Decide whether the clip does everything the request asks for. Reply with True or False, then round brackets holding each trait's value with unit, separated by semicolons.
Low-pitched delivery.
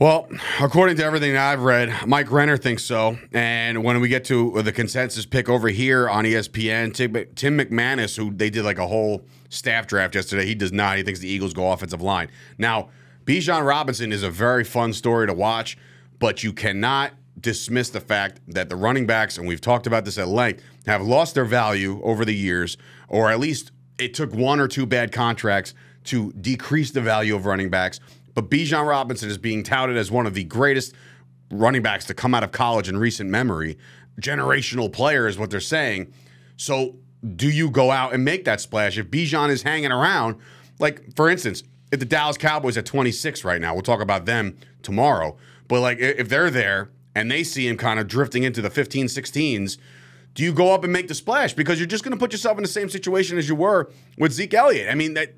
True (120 Hz)